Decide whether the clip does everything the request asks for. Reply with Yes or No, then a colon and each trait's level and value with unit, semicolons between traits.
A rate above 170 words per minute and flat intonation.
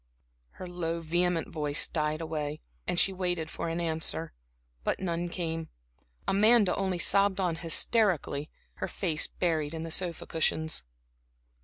No: average, 140 wpm; narrow, 2.2 semitones